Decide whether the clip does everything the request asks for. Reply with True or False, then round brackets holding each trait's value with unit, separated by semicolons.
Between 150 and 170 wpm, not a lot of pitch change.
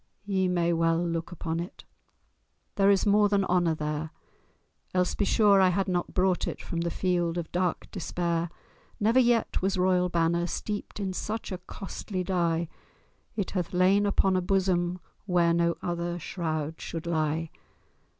True (160 wpm; 2.3 semitones)